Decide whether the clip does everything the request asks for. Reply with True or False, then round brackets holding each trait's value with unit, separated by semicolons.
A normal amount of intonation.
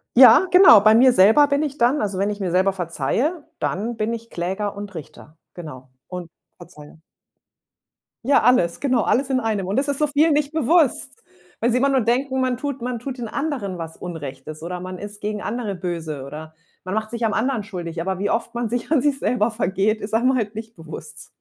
False (6.1 semitones)